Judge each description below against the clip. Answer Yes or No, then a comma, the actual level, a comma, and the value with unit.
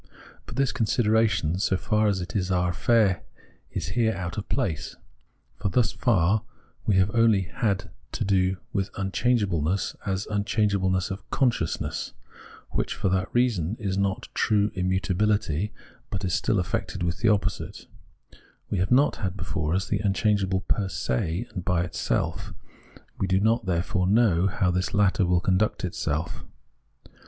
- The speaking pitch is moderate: No, very low, 95 Hz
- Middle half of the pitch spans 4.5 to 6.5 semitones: No, average, 2.7 semitones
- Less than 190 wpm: Yes, average, 155 wpm